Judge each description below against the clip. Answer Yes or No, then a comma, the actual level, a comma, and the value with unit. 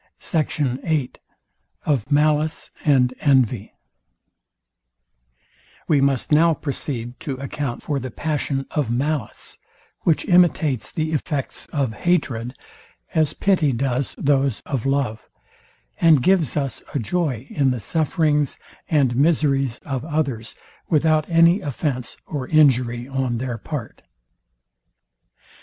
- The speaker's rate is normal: No, slow, 115 wpm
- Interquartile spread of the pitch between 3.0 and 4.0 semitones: Yes, average, 3.5 semitones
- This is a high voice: No, medium, 140 Hz